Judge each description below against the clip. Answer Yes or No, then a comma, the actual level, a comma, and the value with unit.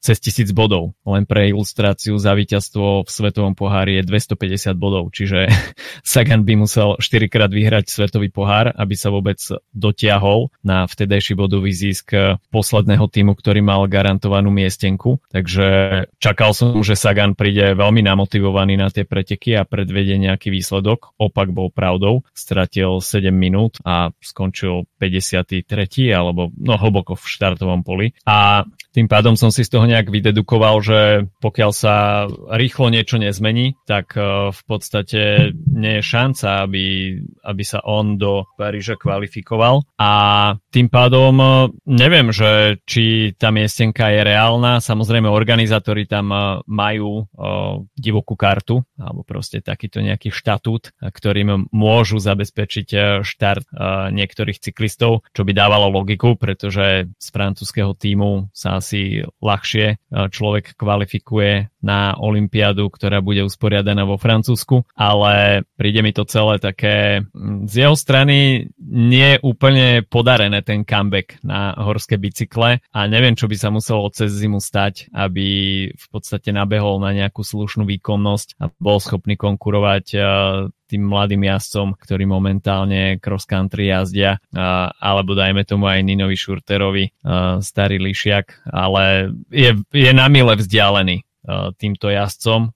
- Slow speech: No, average, 130 wpm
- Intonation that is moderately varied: No, narrow, 2.1 semitones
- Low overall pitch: Yes, low, 105 Hz